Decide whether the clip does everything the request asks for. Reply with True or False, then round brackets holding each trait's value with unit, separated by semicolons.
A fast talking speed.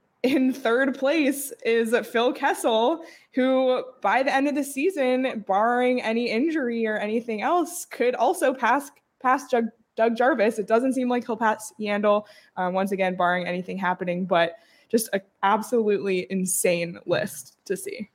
False (155 wpm)